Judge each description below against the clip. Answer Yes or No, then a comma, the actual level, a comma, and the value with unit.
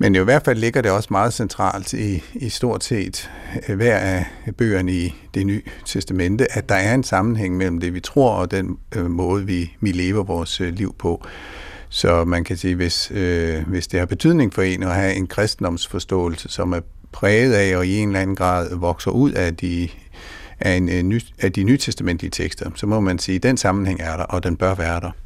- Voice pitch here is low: Yes, very low, 95 Hz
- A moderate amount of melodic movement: No, narrow, 2.3 semitones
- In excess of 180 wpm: Yes, average, 210 wpm